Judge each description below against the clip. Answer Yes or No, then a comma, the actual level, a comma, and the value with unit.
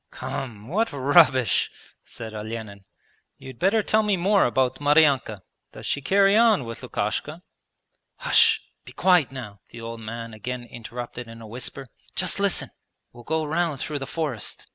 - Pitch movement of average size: No, wide, 6.9 semitones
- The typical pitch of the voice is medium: No, low, 130 Hz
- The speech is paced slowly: No, average, 155 wpm